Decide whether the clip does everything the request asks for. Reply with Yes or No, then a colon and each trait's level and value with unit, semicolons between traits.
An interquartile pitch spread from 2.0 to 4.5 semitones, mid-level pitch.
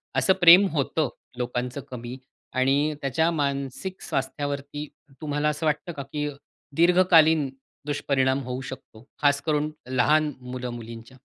Yes: average, 2.9 semitones; medium, 145 Hz